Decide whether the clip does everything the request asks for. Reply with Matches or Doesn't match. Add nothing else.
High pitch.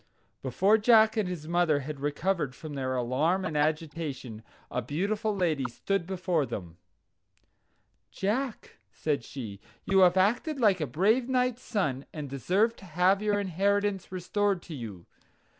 Doesn't match